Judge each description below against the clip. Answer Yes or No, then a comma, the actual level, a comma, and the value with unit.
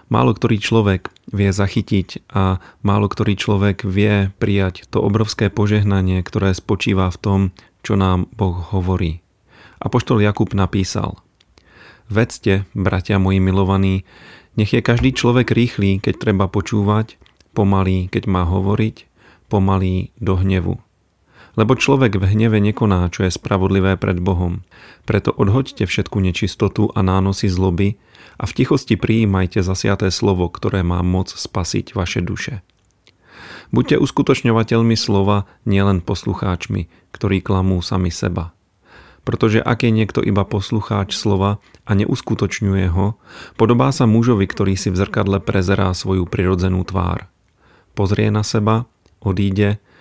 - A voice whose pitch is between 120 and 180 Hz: No, low, 100 Hz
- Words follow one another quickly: No, average, 130 wpm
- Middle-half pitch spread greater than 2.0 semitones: Yes, narrow, 2.6 semitones